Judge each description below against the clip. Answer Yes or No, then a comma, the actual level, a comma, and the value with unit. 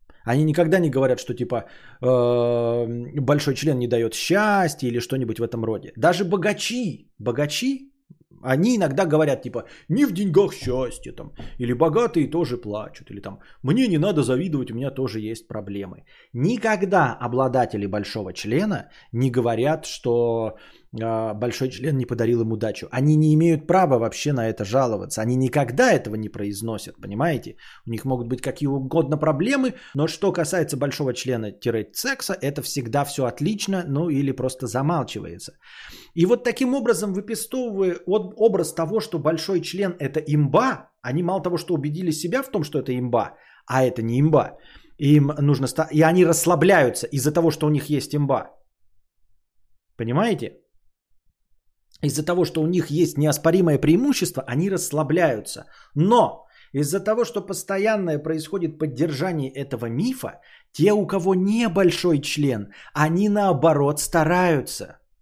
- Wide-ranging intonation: Yes, wide, 6.2 semitones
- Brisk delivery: No, average, 145 wpm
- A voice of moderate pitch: Yes, medium, 145 Hz